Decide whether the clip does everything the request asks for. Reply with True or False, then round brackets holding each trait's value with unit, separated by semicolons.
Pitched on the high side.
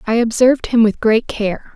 True (225 Hz)